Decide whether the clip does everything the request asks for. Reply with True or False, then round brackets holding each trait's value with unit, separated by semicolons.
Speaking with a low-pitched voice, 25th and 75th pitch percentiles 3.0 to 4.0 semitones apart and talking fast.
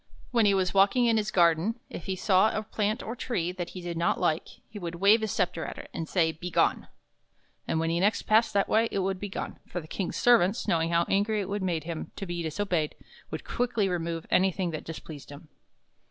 False (185 Hz; 3.7 semitones; 235 wpm)